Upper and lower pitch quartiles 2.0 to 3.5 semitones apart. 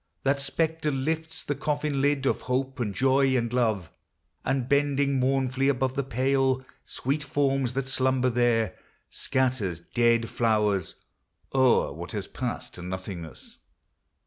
Yes: average, 2.7 semitones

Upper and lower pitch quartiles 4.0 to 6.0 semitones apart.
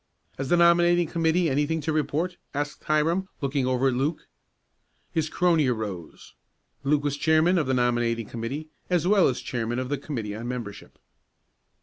Yes: average, 4.8 semitones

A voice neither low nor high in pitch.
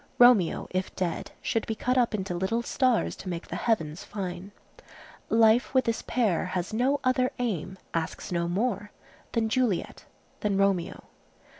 No: high, 210 Hz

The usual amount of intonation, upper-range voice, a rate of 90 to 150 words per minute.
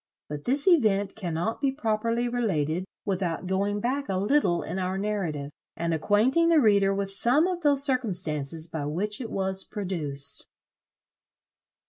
No: wide, 5.8 semitones; high, 200 Hz; average, 145 wpm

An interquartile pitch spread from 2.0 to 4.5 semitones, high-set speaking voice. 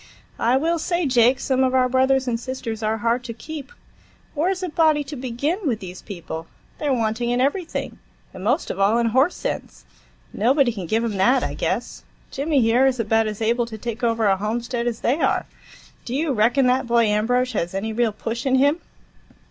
Yes: average, 3.3 semitones; high, 245 Hz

